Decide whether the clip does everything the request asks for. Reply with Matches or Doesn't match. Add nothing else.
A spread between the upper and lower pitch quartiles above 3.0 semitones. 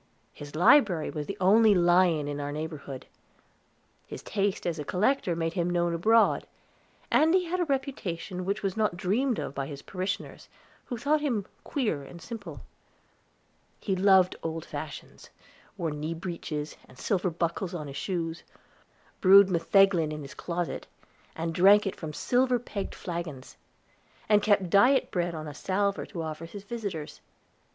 Matches